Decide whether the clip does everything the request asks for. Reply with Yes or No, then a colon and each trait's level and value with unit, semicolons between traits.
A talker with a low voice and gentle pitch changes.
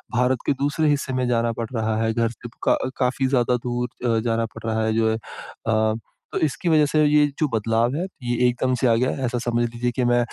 Yes: low, 120 Hz; narrow, 2.2 semitones